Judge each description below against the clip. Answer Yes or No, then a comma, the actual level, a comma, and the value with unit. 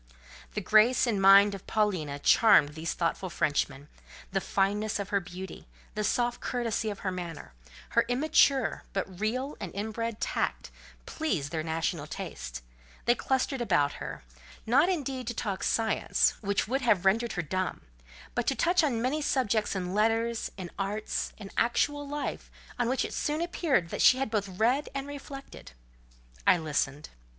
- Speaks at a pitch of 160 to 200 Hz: No, high, 215 Hz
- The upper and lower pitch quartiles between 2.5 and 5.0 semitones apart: No, wide, 5.4 semitones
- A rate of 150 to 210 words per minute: Yes, average, 160 wpm